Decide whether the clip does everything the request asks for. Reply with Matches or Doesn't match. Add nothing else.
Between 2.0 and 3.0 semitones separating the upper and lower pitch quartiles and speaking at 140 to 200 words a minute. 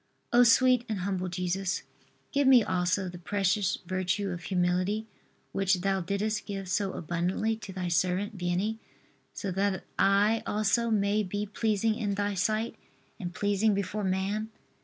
Matches